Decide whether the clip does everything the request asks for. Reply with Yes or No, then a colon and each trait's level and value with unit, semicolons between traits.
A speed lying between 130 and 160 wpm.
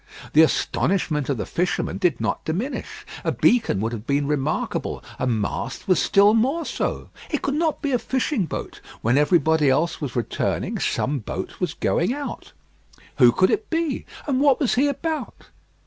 No: average, 175 wpm